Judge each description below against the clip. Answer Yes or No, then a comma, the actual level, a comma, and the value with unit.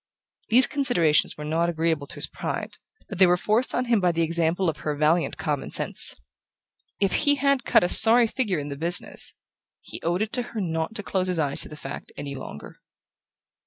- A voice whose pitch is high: No, medium, 175 Hz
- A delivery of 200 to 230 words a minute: Yes, fast, 205 wpm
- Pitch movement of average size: No, wide, 5.8 semitones